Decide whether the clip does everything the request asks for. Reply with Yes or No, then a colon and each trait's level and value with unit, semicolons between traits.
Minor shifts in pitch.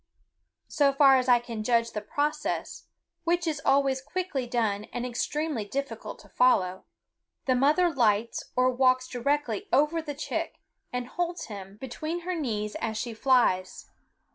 No: average, 4.1 semitones